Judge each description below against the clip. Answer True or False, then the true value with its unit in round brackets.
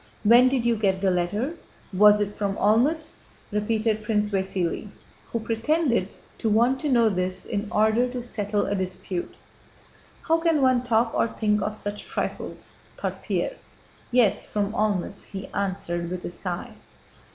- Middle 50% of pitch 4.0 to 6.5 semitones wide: False (3.2 semitones)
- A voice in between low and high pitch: False (210 Hz)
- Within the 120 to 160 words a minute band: True (155 wpm)